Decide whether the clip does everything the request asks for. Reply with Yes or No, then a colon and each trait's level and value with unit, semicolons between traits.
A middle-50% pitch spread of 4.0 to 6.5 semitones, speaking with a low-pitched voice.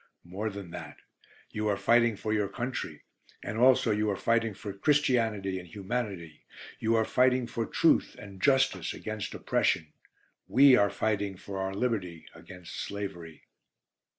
No: average, 3.4 semitones; low, 105 Hz